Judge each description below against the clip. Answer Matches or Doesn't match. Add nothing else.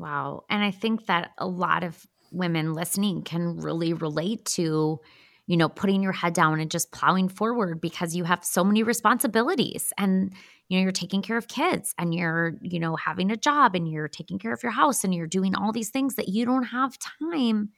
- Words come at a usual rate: Doesn't match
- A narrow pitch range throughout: Doesn't match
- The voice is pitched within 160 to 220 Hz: Matches